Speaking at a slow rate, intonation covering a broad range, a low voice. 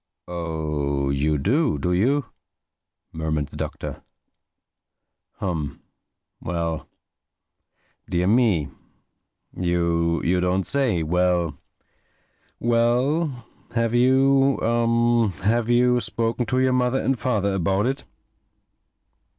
Yes: slow, 75 wpm; wide, 6.7 semitones; low, 100 Hz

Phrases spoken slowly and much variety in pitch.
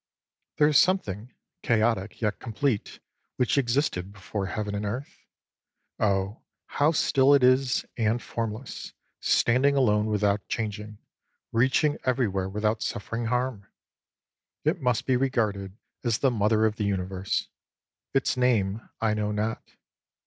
No: slow, 130 wpm; average, 3.6 semitones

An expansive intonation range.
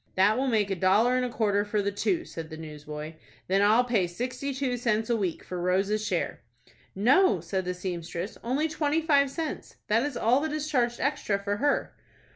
Yes: wide, 5.8 semitones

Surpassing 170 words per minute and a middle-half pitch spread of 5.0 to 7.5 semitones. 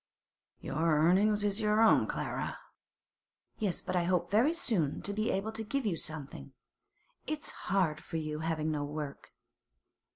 No: average, 155 wpm; wide, 5.4 semitones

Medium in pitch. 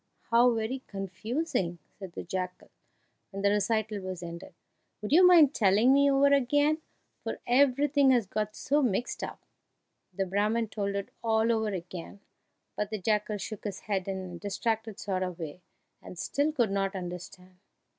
No: high, 210 Hz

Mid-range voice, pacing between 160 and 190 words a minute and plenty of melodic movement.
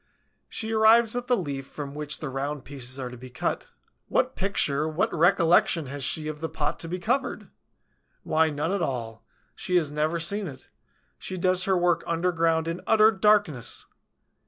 No: medium, 165 Hz; average, 180 wpm; average, 4.6 semitones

